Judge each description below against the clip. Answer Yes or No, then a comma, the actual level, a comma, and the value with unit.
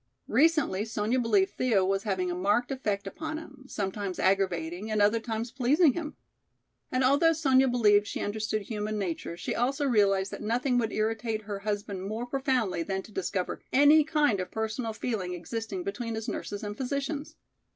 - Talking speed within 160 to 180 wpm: Yes, average, 175 wpm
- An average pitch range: Yes, average, 4.4 semitones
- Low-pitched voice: No, high, 220 Hz